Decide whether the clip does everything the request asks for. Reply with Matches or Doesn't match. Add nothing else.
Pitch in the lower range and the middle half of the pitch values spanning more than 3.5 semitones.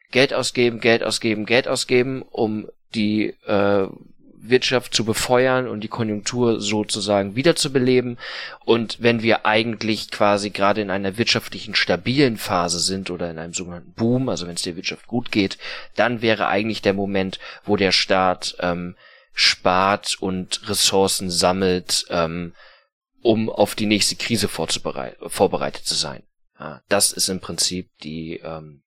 Matches